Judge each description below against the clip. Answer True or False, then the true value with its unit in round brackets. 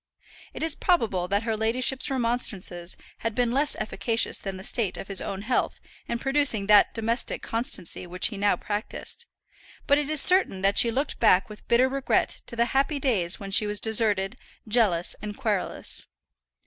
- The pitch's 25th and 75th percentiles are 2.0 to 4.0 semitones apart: False (4.4 semitones)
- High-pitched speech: True (225 Hz)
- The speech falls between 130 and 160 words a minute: False (175 wpm)